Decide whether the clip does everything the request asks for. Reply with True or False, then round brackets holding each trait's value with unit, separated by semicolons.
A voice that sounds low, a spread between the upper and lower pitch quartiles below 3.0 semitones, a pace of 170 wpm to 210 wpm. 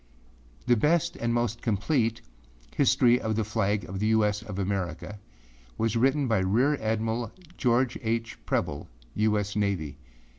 False (110 Hz; 2.5 semitones; 150 wpm)